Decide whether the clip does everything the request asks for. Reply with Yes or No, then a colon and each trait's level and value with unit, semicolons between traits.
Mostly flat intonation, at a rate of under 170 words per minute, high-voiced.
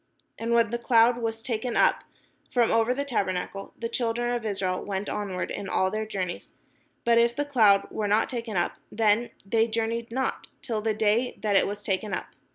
No: narrow, 2.3 semitones; average, 195 wpm; high, 225 Hz